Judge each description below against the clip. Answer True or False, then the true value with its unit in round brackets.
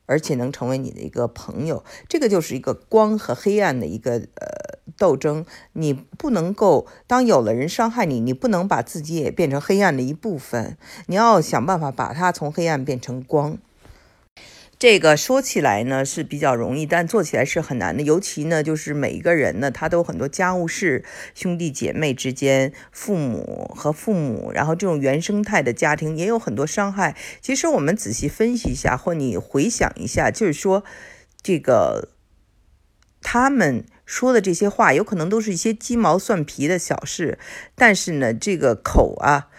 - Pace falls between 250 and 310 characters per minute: True (270 characters per minute)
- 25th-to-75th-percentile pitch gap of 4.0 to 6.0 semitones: False (7.6 semitones)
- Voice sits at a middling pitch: True (165 Hz)